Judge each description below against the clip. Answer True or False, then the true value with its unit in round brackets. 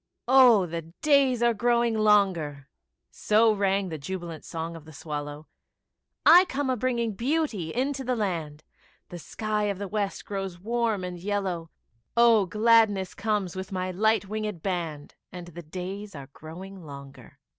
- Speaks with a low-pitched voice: False (195 Hz)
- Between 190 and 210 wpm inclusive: False (155 wpm)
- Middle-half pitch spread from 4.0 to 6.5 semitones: True (5.0 semitones)